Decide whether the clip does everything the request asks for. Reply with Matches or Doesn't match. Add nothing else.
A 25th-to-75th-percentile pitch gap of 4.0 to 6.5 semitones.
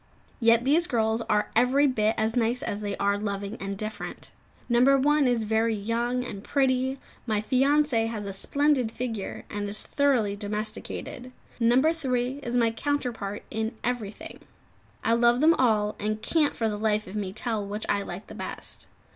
Doesn't match